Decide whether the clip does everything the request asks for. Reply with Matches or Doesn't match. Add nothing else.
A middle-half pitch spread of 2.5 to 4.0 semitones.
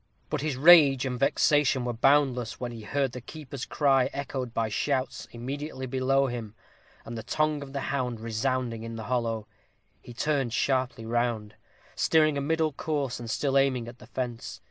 Matches